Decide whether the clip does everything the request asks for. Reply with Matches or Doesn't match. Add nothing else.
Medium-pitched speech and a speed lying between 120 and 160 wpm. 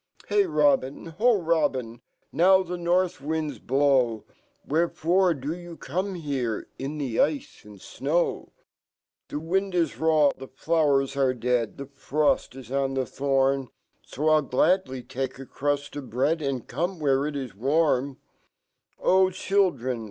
Matches